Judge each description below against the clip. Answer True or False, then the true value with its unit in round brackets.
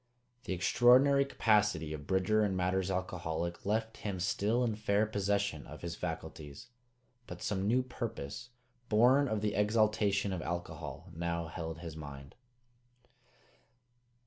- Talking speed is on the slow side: True (130 wpm)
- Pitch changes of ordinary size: True (4.1 semitones)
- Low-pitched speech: True (100 Hz)